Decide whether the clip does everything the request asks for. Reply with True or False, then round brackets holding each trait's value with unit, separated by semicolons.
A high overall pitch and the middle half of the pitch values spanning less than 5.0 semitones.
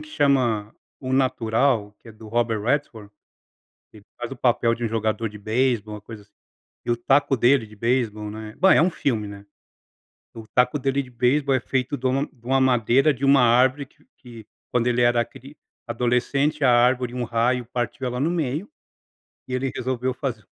False (125 Hz; 2.9 semitones)